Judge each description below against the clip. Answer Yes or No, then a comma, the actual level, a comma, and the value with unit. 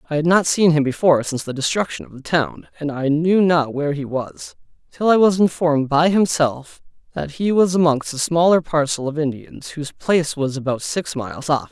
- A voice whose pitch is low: No, medium, 155 Hz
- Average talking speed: No, fast, 210 wpm